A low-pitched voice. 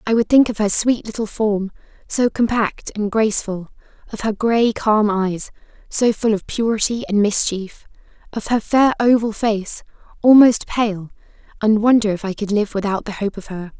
No: high, 215 Hz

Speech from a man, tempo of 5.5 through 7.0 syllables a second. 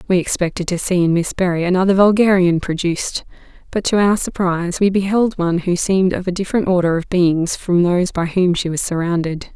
No: female; 5.8 syllables/s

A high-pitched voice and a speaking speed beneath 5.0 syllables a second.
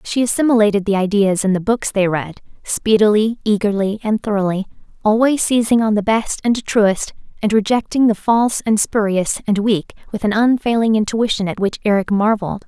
No: high, 210 Hz; 5.3 syllables/s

